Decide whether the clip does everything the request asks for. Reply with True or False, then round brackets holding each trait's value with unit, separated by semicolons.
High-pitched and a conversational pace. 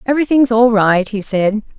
True (225 Hz; 170 wpm)